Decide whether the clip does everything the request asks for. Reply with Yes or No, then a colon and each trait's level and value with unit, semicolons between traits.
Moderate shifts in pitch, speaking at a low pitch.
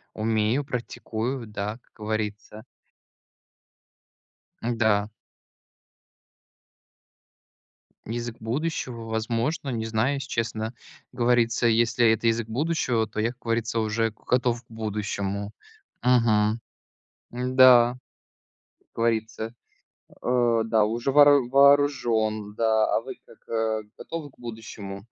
No: narrow, 2.1 semitones; low, 115 Hz